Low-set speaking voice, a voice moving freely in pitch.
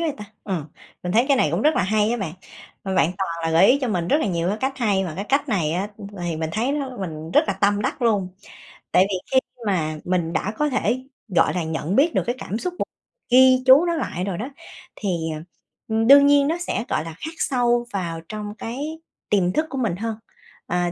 No: high, 210 Hz; wide, 6.5 semitones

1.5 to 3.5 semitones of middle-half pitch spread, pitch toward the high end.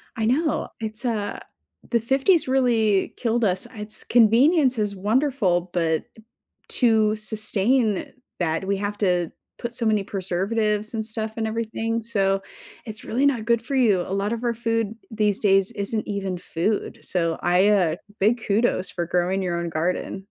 Yes: average, 3.1 semitones; high, 215 Hz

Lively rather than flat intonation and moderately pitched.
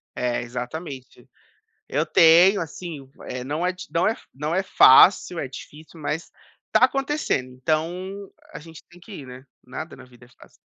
Yes: wide, 5.7 semitones; medium, 160 Hz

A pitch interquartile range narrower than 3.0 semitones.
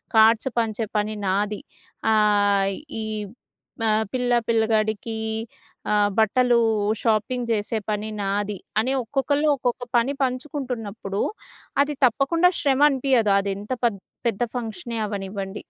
No: average, 3.4 semitones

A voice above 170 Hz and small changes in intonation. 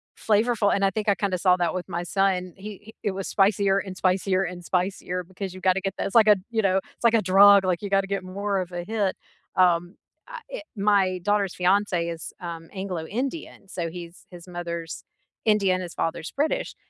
Yes: high, 190 Hz; narrow, 2.2 semitones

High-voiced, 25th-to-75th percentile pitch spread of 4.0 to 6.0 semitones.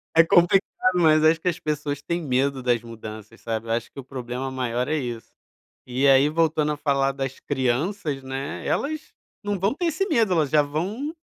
No: medium, 145 Hz; average, 4.9 semitones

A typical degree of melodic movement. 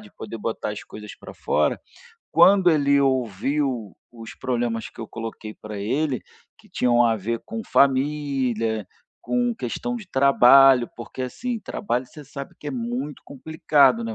Yes: average, 4.4 semitones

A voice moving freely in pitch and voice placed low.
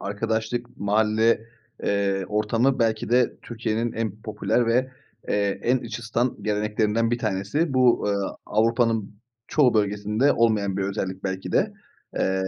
No: narrow, 2.4 semitones; low, 110 Hz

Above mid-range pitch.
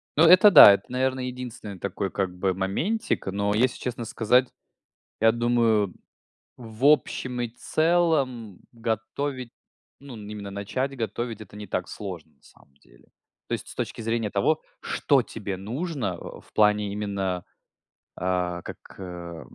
No: low, 110 Hz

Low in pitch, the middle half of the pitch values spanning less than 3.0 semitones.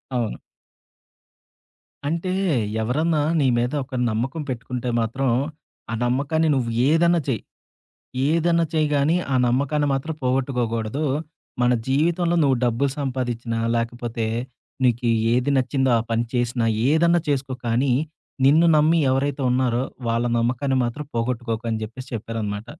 No: low, 130 Hz; average, 3.6 semitones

